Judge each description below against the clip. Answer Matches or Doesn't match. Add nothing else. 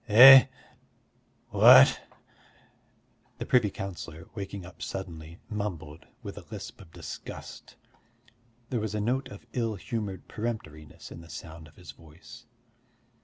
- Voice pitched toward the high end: Doesn't match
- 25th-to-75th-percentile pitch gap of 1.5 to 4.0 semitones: Doesn't match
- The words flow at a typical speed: Doesn't match